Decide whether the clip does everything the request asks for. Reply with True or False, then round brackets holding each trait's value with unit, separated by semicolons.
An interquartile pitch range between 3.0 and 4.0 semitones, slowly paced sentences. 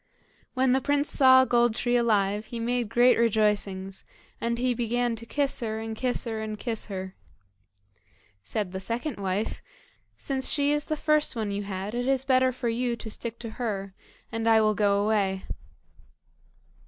False (3.3 semitones; 175 wpm)